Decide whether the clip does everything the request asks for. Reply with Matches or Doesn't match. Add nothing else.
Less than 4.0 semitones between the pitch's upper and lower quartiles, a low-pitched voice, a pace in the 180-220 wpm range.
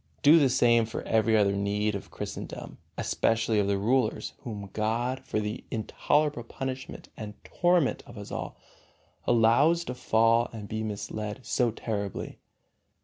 Doesn't match